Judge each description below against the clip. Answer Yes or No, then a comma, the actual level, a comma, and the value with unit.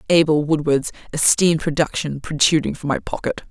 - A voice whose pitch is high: No, medium, 155 Hz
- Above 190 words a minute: No, slow, 135 wpm